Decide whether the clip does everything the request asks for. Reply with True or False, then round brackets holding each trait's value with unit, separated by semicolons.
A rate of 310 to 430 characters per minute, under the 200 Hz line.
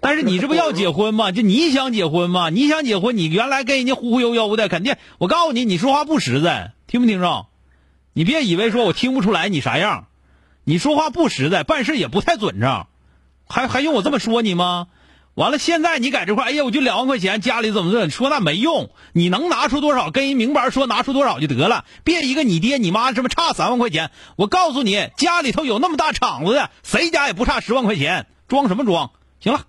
False (340 characters per minute; 255 Hz)